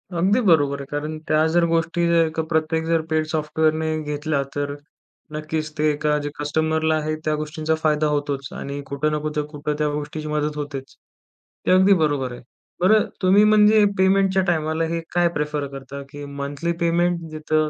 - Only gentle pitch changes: Yes, narrow, 2.1 semitones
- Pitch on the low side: No, medium, 155 Hz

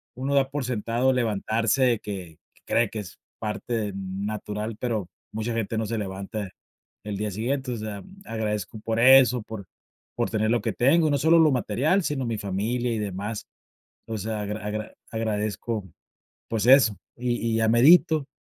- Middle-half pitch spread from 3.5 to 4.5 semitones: No, average, 2.9 semitones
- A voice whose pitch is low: Yes, low, 110 Hz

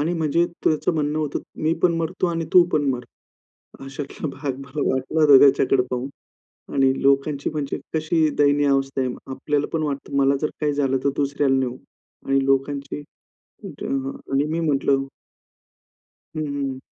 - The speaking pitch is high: No, medium, 140 Hz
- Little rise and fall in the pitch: Yes, narrow, 2.0 semitones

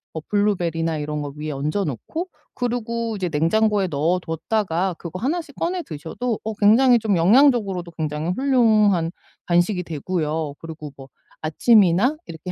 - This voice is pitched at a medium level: Yes, medium, 180 Hz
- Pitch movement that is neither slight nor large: No, wide, 5.7 semitones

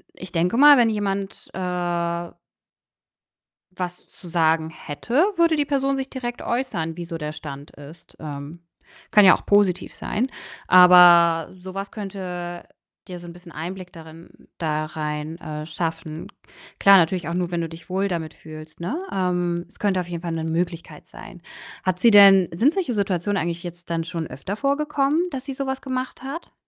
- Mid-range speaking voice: Yes, medium, 180 Hz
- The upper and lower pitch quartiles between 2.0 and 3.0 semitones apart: No, average, 3.7 semitones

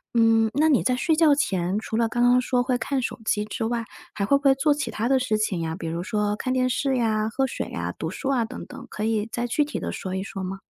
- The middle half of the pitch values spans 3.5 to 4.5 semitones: Yes, average, 3.9 semitones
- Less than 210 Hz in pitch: No, high, 235 Hz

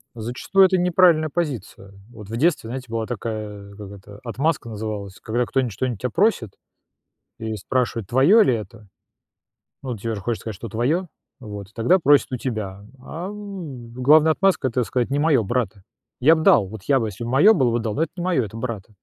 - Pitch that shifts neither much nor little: No, wide, 6.0 semitones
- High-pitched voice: No, low, 120 Hz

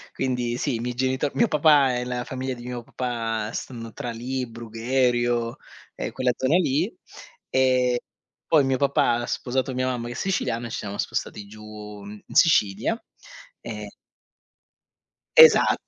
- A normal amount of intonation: No, narrow, 2.2 semitones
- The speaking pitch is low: Yes, low, 125 Hz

